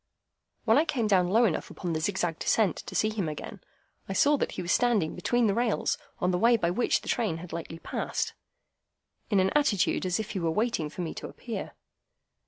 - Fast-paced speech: Yes, fast, 215 wpm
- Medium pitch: No, high, 195 Hz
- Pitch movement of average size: Yes, average, 4.8 semitones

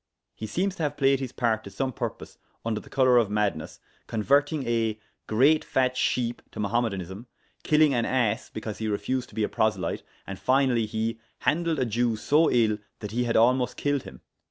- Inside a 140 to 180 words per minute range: No, average, 190 wpm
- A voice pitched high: No, low, 120 Hz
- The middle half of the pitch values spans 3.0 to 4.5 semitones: Yes, average, 3.5 semitones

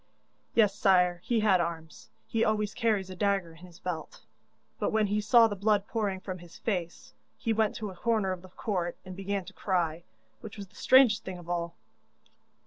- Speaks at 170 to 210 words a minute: Yes, average, 200 wpm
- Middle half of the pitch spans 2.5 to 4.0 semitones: Yes, average, 3.2 semitones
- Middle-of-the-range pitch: No, high, 195 Hz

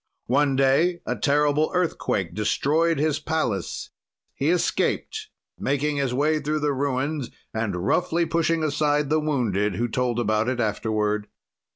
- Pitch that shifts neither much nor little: Yes, average, 4.7 semitones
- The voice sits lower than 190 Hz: Yes, medium, 140 Hz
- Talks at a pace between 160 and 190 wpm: No, average, 140 wpm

